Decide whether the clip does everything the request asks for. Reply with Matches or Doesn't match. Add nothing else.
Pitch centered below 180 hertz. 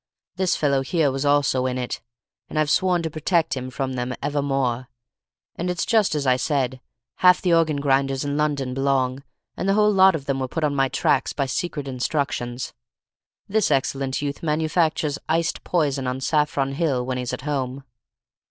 Matches